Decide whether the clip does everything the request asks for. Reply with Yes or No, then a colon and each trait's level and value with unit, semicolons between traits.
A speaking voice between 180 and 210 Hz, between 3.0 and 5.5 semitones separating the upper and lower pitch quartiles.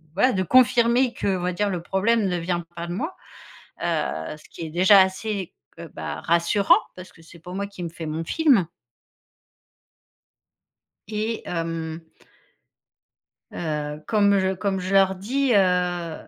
Yes: medium, 185 Hz; average, 3.3 semitones